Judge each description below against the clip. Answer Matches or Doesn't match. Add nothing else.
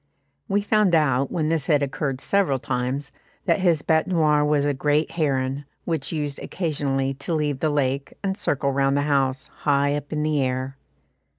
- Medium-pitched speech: Matches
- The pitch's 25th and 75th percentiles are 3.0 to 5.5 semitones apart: Doesn't match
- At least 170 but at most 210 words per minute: Matches